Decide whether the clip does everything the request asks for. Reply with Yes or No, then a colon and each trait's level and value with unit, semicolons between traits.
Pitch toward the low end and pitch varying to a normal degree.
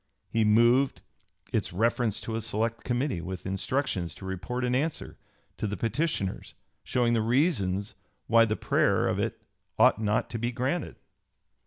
Yes: low, 115 Hz; average, 3.3 semitones